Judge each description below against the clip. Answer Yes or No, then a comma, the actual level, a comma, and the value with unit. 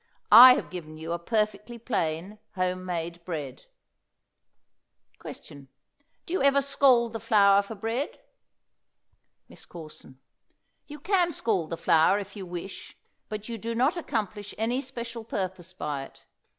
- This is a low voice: No, high, 205 Hz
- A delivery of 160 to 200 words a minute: No, average, 140 wpm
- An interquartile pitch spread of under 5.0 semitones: No, wide, 5.4 semitones